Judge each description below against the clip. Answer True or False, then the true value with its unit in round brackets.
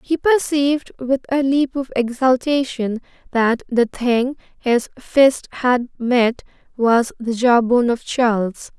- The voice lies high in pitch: True (250 Hz)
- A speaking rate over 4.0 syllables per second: False (3.8 syllables/s)